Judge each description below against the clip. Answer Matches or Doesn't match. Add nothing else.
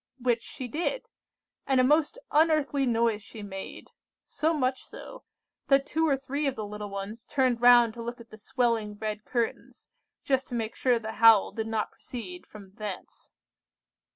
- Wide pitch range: Doesn't match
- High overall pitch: Matches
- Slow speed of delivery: Doesn't match